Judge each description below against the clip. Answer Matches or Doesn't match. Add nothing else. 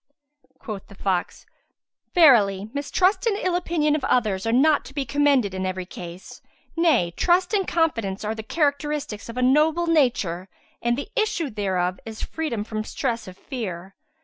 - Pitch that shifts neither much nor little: Doesn't match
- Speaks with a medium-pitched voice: Doesn't match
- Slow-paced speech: Doesn't match